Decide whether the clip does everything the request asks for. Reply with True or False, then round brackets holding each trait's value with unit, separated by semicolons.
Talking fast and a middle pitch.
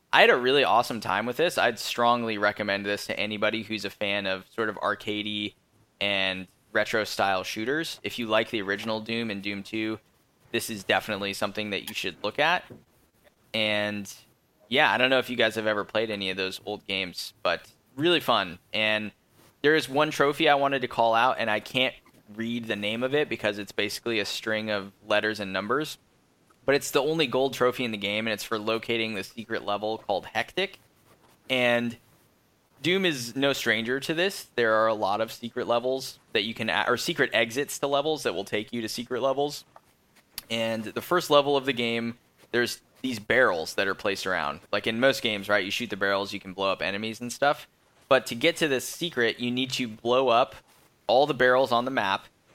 False (210 wpm; 115 Hz)